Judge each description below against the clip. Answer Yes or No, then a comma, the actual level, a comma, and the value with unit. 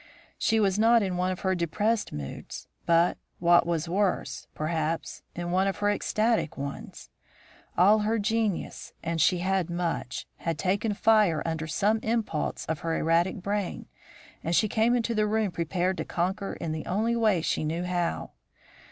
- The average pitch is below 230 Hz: Yes, medium, 185 Hz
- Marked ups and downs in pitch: No, average, 4.1 semitones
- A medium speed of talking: Yes, average, 170 wpm